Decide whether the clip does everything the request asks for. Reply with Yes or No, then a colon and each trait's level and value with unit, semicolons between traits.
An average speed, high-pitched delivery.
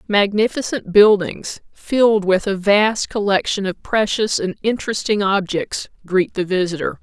No: slow, 130 wpm; high, 200 Hz